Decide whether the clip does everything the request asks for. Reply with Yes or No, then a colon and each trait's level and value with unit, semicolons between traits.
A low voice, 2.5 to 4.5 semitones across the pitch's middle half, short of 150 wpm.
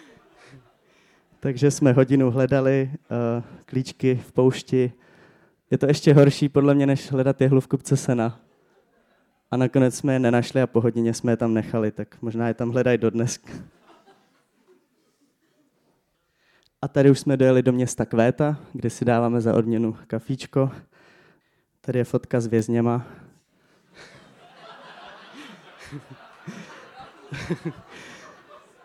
Yes: low, 130 Hz; average, 2.8 semitones; average, 120 wpm